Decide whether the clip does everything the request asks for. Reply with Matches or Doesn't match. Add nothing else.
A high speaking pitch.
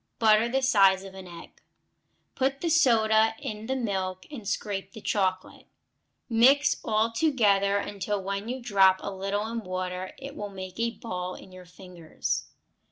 Matches